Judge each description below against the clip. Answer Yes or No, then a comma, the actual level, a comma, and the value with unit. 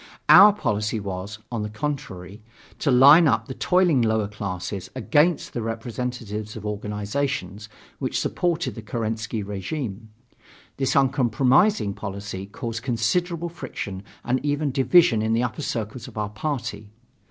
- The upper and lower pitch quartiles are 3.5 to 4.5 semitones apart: No, average, 4.9 semitones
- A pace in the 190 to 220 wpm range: No, slow, 135 wpm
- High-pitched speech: No, low, 115 Hz